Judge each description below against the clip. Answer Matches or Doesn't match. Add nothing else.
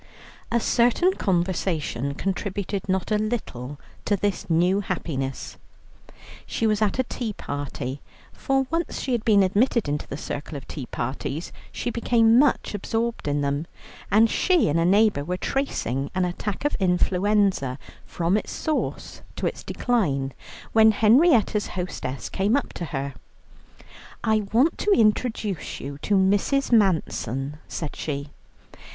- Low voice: Doesn't match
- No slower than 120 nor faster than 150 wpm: Matches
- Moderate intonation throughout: Doesn't match